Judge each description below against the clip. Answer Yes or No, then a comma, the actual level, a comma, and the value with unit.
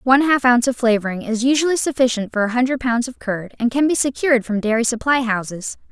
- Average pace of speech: No, fast, 225 wpm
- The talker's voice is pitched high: Yes, high, 245 Hz